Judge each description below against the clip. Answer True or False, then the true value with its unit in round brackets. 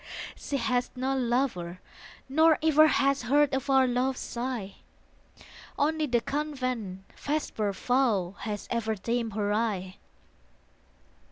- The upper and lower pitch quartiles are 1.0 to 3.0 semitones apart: False (4.3 semitones)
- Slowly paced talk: True (110 wpm)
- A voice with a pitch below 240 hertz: False (250 Hz)